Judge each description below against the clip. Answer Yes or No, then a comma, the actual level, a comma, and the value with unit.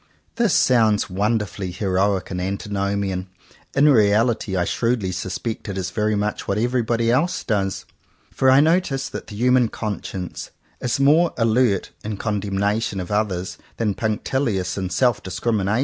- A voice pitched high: No, low, 105 Hz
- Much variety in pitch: No, average, 3.7 semitones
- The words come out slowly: No, average, 150 wpm